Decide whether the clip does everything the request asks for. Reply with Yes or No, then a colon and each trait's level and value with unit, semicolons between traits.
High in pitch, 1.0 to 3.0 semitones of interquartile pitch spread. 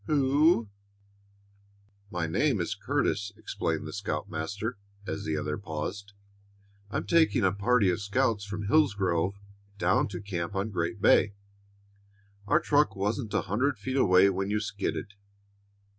No: low, 100 Hz; narrow, 2.4 semitones